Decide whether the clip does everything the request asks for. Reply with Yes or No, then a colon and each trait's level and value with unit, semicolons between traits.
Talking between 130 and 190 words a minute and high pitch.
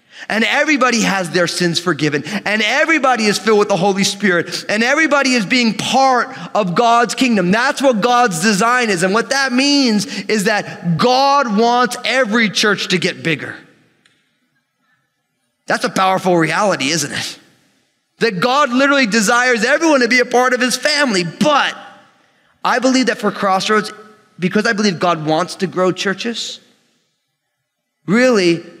Yes: average, 150 wpm; high, 220 Hz